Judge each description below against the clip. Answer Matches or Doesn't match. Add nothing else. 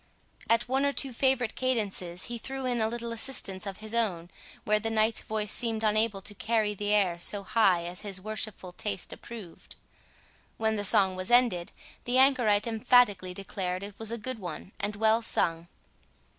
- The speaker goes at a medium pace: Matches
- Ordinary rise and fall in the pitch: Matches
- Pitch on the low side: Doesn't match